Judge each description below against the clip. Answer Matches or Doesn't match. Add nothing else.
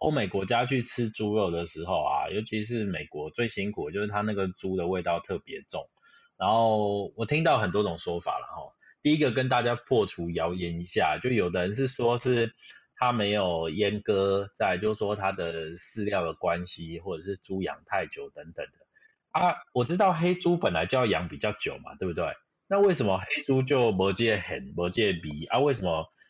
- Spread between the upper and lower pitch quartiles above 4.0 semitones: Matches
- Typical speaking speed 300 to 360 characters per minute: Doesn't match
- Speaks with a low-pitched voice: Matches